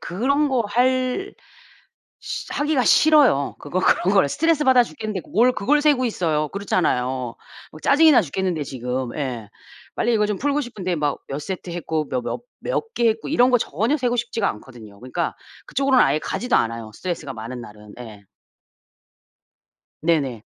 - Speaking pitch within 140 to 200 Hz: Yes, high, 190 Hz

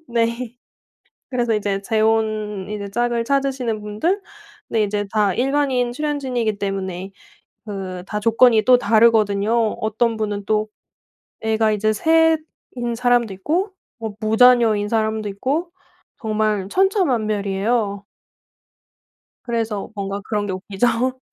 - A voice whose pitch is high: Yes, high, 220 Hz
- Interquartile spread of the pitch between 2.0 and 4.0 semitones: Yes, average, 2.9 semitones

